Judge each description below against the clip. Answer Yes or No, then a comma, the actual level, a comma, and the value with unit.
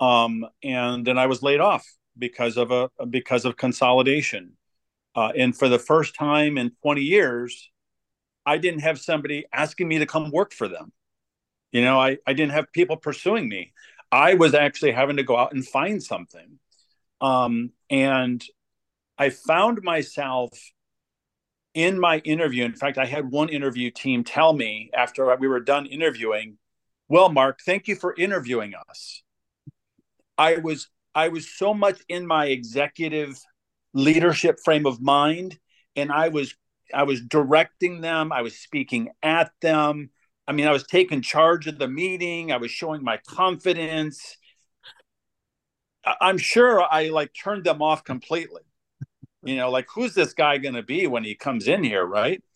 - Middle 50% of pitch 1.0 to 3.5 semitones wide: No, average, 3.9 semitones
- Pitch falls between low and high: Yes, medium, 145 Hz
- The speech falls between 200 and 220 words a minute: No, average, 165 wpm